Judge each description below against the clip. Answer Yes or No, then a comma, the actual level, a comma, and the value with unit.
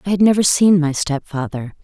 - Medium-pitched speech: Yes, medium, 170 Hz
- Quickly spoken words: No, average, 195 wpm